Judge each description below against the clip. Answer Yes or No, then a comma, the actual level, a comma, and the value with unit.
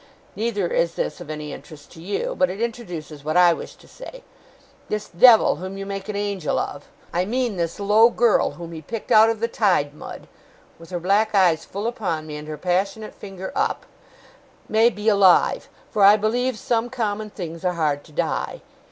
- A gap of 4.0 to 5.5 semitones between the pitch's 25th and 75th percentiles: Yes, average, 4.6 semitones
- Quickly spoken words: No, average, 195 wpm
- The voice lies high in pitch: Yes, high, 195 Hz